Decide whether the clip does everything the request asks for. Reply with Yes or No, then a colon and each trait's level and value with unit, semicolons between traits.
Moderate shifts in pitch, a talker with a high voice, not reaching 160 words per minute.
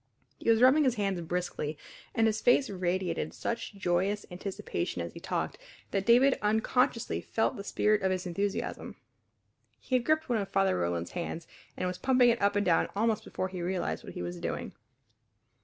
No: average, 4.1 semitones; high, 200 Hz; average, 185 wpm